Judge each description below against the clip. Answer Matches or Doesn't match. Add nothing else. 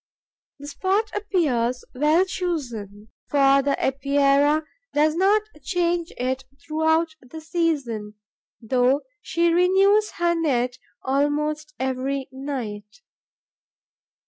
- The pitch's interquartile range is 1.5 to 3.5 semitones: Doesn't match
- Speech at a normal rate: Doesn't match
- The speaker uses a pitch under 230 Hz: Doesn't match